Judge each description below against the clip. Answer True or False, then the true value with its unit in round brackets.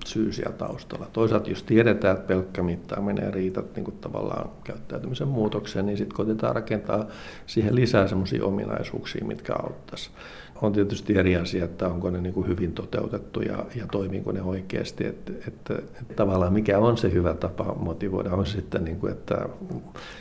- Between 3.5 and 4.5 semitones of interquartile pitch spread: False (2.5 semitones)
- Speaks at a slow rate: False (155 wpm)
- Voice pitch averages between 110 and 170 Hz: False (100 Hz)